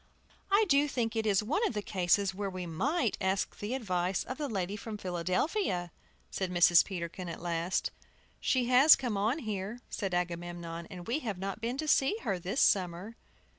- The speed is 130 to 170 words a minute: No, average, 185 wpm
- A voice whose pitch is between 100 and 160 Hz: No, high, 200 Hz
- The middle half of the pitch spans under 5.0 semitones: No, wide, 5.4 semitones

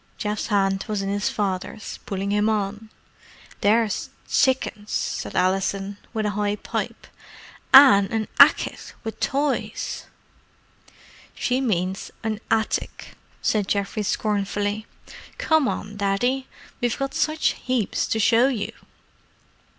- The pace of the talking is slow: Yes, slow, 120 wpm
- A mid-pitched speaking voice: No, high, 210 Hz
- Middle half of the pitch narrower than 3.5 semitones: Yes, average, 2.8 semitones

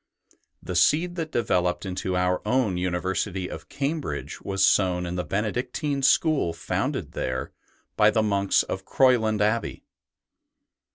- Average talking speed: No, slow, 130 wpm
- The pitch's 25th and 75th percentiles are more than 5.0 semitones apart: Yes, wide, 5.5 semitones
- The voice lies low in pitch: Yes, low, 100 Hz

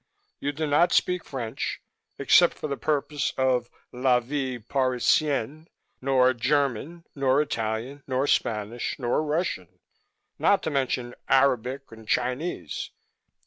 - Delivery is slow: Yes, slow, 120 wpm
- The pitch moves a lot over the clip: No, average, 3.0 semitones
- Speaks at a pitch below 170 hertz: Yes, low, 135 Hz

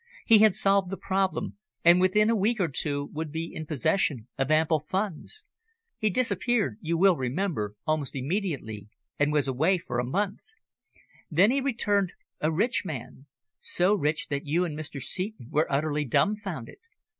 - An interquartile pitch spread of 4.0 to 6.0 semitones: Yes, wide, 5.5 semitones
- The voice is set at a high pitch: No, medium, 165 Hz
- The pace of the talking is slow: No, average, 165 wpm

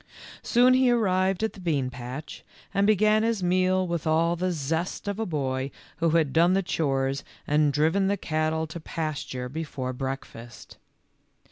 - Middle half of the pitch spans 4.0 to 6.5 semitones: Yes, average, 5.0 semitones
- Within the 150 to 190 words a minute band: Yes, average, 170 wpm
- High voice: No, medium, 165 Hz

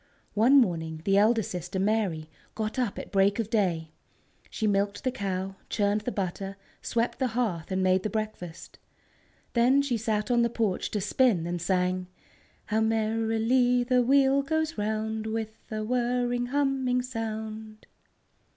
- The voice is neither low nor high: No, high, 220 Hz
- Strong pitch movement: No, average, 3.9 semitones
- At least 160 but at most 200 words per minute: No, average, 150 wpm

